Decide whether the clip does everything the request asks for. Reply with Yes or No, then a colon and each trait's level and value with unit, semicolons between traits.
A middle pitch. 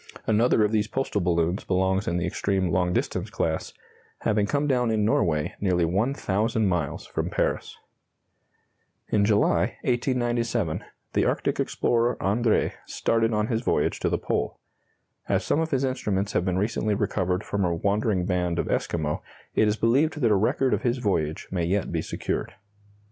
No: low, 105 Hz